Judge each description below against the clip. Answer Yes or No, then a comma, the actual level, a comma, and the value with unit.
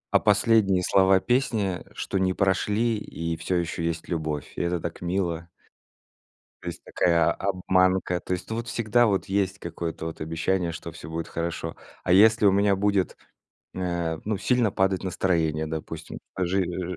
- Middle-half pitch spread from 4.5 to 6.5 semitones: No, average, 2.9 semitones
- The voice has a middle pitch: No, very low, 95 Hz